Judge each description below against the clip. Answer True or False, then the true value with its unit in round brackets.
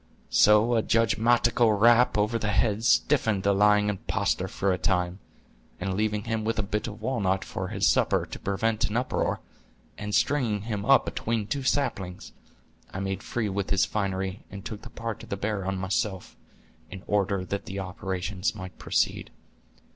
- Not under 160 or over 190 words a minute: True (170 wpm)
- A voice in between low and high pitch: False (105 Hz)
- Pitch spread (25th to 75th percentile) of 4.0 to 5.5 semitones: False (2.6 semitones)